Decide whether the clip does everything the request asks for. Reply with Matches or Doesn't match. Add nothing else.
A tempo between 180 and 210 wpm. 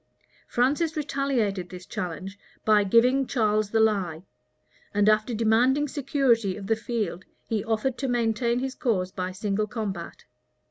Doesn't match